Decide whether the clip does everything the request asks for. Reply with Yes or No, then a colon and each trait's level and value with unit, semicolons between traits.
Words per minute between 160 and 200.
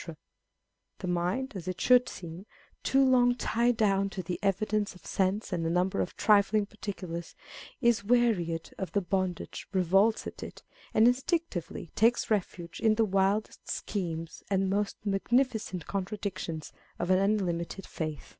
No: average, 145 wpm